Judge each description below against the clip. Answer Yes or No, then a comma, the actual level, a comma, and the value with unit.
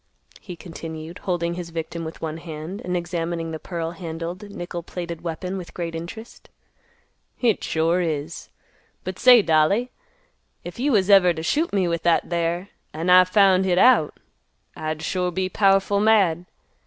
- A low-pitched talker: No, medium, 175 Hz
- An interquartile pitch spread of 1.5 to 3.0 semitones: Yes, narrow, 2.4 semitones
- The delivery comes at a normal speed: Yes, average, 160 wpm